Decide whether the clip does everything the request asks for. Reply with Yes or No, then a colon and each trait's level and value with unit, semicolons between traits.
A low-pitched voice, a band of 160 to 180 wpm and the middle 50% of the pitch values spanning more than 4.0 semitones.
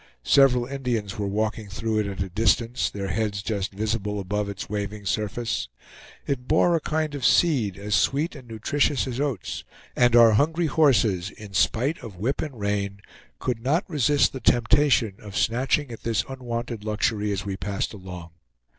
Yes: low, 110 Hz; average, 170 wpm; average, 4.6 semitones